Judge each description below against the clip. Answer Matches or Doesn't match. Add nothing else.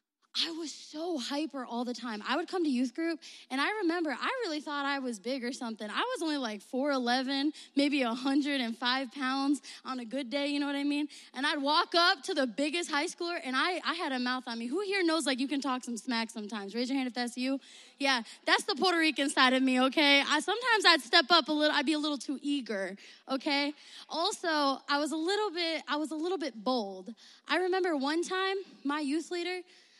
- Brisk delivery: Matches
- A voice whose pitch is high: Matches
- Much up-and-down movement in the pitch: Doesn't match